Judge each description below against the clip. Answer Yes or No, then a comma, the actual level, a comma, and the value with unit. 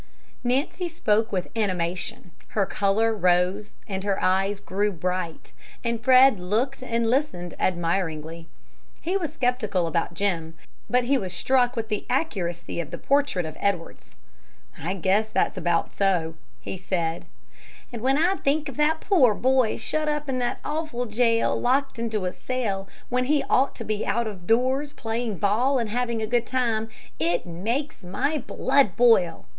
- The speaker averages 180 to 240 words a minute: No, average, 160 wpm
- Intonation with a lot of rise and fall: Yes, wide, 5.7 semitones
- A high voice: Yes, high, 220 Hz